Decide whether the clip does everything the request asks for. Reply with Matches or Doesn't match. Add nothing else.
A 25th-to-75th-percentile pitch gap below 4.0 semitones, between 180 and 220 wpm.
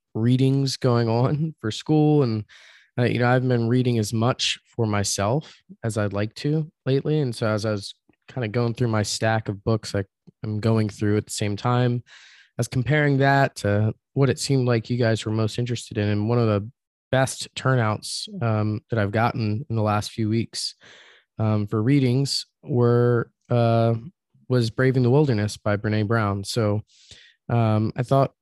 Matches